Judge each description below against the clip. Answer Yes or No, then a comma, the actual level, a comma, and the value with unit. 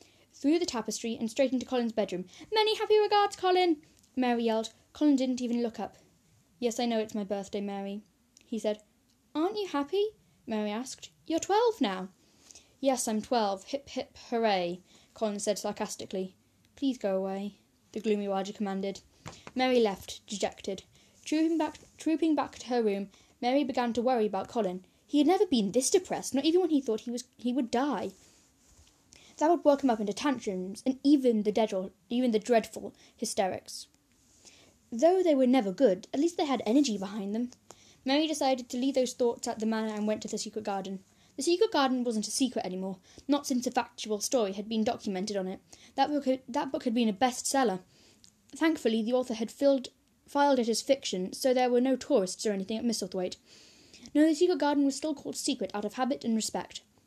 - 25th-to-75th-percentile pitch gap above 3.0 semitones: Yes, average, 4.7 semitones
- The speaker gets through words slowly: No, average, 195 wpm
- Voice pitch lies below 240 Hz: No, high, 245 Hz